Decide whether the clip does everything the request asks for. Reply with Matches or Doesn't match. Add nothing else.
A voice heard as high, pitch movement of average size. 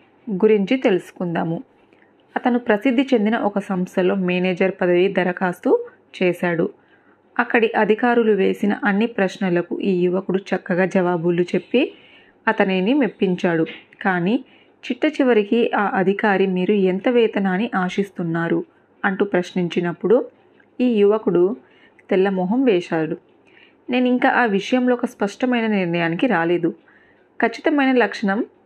Matches